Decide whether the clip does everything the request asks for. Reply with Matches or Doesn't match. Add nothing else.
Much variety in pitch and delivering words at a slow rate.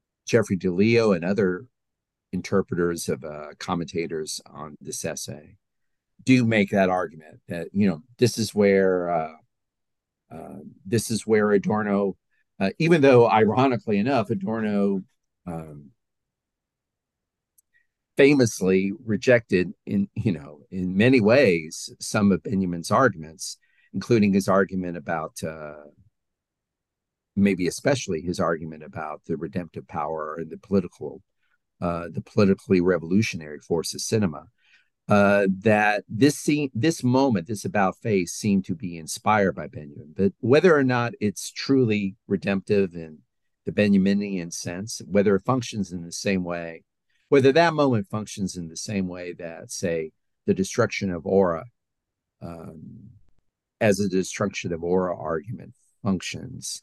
Doesn't match